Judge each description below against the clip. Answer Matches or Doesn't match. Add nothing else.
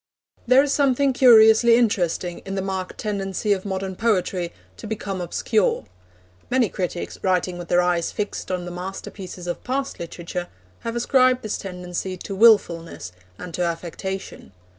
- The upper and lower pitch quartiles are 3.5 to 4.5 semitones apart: Matches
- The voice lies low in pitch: Doesn't match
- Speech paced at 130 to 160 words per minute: Matches